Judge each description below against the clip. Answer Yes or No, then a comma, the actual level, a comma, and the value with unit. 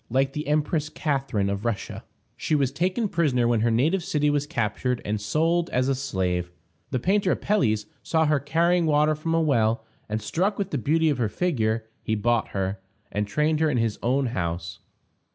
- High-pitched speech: No, low, 135 Hz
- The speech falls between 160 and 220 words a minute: Yes, average, 190 wpm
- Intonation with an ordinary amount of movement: No, wide, 6.3 semitones